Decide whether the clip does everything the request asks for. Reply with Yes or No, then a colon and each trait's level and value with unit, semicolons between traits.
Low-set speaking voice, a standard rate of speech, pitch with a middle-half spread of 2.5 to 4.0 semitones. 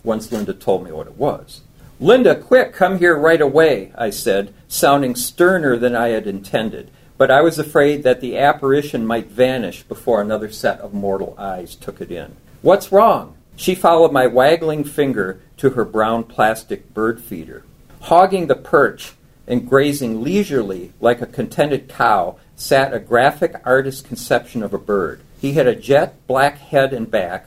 No: low, 130 Hz; average, 170 wpm; average, 4.5 semitones